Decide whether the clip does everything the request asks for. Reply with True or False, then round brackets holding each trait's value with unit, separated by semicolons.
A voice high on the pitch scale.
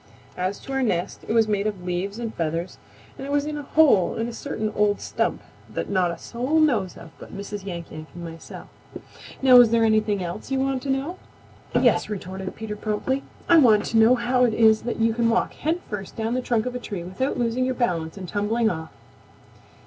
True (220 Hz)